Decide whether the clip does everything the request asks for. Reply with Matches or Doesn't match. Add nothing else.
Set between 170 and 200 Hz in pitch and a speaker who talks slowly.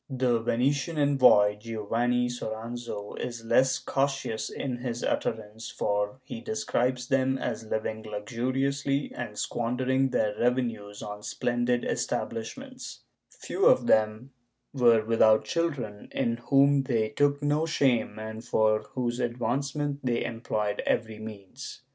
Doesn't match